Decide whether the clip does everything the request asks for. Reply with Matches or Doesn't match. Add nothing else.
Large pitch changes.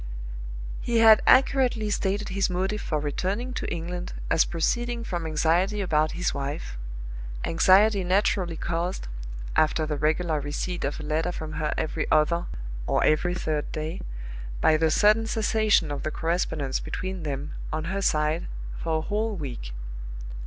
Doesn't match